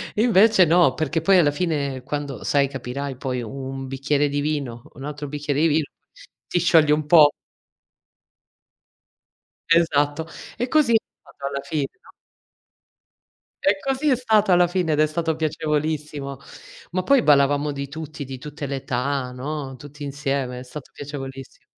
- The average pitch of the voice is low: No, medium, 145 Hz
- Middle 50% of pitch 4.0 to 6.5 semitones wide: No, average, 2.8 semitones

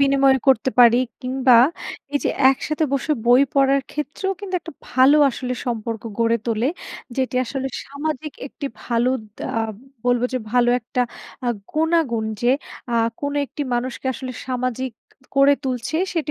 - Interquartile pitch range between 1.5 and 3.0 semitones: Yes, narrow, 2.5 semitones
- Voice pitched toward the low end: No, very high, 260 Hz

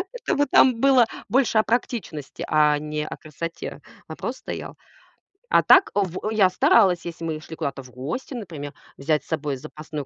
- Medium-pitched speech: Yes, medium, 165 Hz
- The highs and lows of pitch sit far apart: Yes, wide, 7.1 semitones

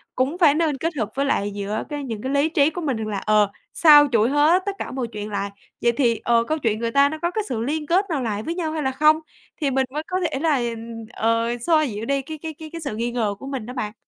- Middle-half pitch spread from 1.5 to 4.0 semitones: No, wide, 5.4 semitones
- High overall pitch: Yes, very high, 270 Hz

